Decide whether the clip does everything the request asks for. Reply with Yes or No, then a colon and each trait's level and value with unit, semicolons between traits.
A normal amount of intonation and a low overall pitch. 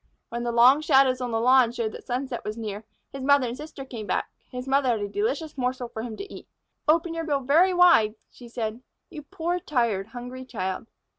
No: average, 3.6 semitones; very high, 255 Hz